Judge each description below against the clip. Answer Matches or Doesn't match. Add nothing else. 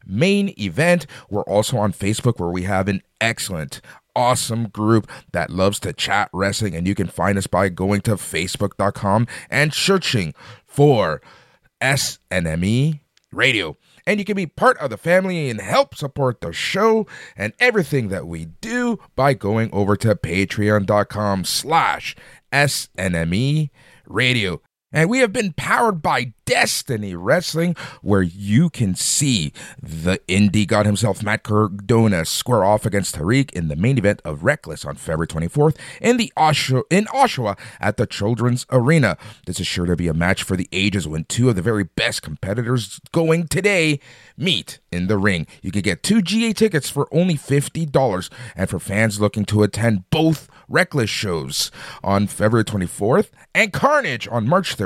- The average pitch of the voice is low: Matches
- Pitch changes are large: Matches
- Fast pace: Doesn't match